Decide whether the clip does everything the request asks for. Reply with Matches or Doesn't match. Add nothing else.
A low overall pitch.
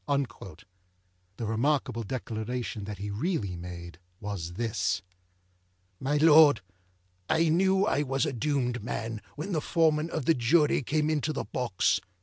Matches